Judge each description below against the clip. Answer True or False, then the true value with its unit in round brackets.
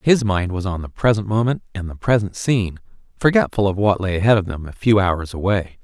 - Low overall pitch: True (100 Hz)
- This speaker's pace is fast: True (225 wpm)